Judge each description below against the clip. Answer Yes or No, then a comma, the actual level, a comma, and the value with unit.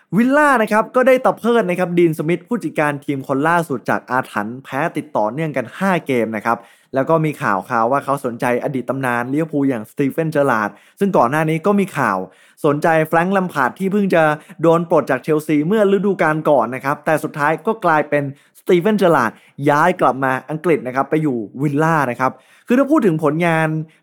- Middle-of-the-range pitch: Yes, medium, 155 Hz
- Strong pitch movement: No, average, 4.5 semitones